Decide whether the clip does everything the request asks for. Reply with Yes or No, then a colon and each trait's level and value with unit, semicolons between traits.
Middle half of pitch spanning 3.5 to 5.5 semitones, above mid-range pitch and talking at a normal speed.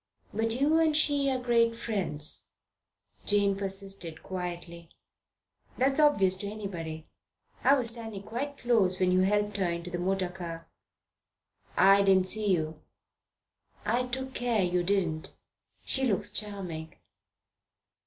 No: average, 4.7 semitones; high, 200 Hz; slow, 130 wpm